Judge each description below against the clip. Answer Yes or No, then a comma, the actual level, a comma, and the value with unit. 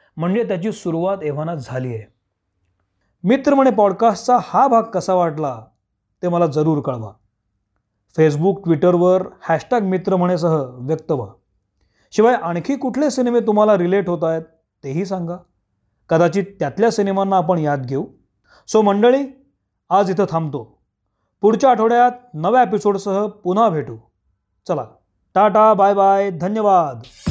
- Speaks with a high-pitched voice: No, medium, 175 Hz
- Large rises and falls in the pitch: Yes, wide, 7.9 semitones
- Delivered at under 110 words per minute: No, average, 125 wpm